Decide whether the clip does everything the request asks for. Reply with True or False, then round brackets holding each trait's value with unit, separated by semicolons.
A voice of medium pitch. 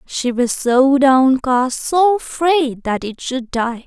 False (265 Hz)